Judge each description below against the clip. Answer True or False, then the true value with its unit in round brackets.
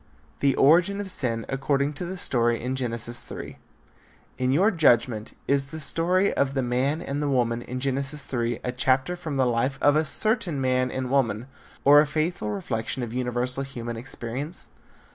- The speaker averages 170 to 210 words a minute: True (180 wpm)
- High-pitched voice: False (135 Hz)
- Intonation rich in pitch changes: False (3.3 semitones)